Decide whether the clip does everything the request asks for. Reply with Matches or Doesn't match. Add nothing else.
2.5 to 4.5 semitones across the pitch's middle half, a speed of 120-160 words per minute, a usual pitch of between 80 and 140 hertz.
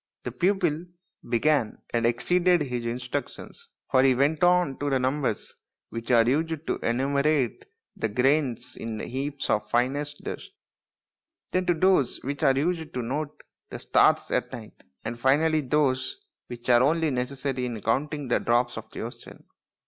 Matches